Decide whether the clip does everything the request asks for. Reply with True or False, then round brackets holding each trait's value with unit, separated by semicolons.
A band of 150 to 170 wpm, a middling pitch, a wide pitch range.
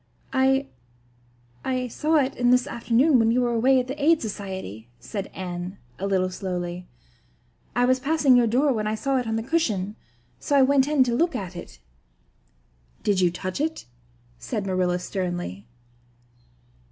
False (165 wpm; 230 Hz; 6.2 semitones)